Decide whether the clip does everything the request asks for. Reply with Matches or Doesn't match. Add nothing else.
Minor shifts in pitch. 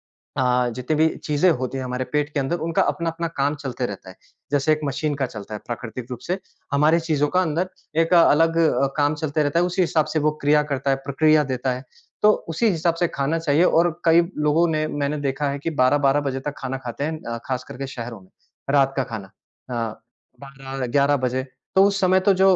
Doesn't match